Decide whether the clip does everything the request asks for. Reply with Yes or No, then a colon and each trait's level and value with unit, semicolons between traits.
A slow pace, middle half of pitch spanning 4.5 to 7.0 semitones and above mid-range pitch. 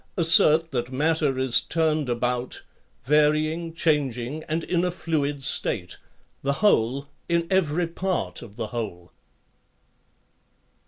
No: slow, 115 wpm; average, 4.8 semitones; medium, 150 Hz